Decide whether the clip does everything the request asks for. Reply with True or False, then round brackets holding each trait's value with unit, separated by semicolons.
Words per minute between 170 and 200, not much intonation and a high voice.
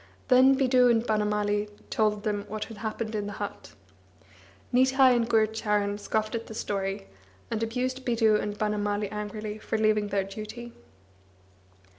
False (145 wpm; 1.9 semitones; 215 Hz)